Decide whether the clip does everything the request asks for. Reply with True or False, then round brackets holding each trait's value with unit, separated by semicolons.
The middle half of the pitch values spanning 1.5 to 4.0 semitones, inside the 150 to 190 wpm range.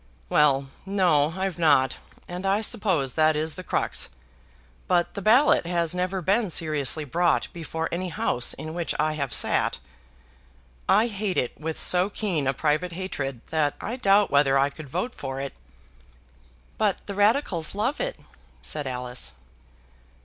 False (4.9 semitones; 155 wpm)